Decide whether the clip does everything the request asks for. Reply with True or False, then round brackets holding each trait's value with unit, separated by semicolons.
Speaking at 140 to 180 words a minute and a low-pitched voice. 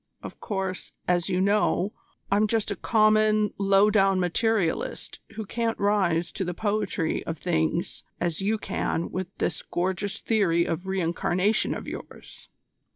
False (150 wpm; 195 Hz)